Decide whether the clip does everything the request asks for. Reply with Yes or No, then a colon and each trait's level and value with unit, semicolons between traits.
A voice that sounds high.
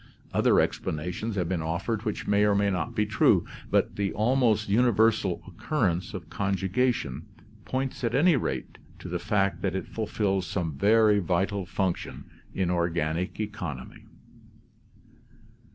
No: low, 100 Hz